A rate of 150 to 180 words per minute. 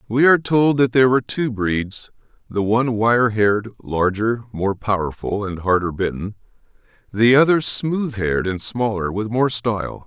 Yes: average, 160 wpm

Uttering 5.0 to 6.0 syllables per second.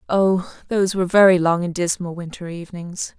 Yes: 5.7 syllables/s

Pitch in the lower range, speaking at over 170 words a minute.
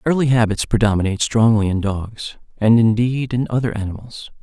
No: low, 115 Hz; average, 150 wpm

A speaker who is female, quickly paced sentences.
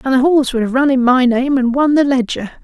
Yes: female; fast, 295 wpm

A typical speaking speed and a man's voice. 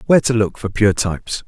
No: fast, 245 wpm; male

